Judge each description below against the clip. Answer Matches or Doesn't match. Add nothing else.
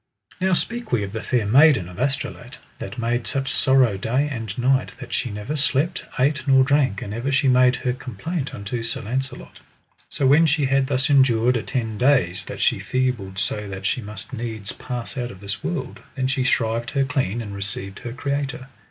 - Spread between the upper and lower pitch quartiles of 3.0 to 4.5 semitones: Matches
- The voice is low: Matches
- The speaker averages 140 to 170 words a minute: Doesn't match